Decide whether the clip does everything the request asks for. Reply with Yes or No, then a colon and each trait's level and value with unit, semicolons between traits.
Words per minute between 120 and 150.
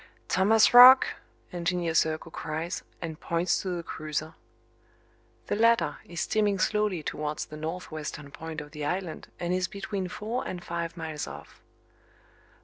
Yes: average, 140 wpm